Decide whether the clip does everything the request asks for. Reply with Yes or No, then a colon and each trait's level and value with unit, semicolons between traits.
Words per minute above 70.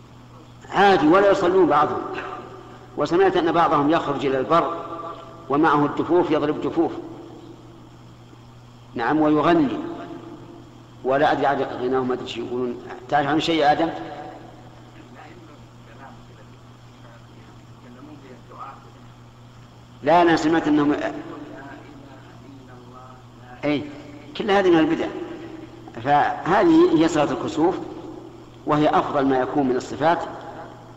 Yes: average, 85 wpm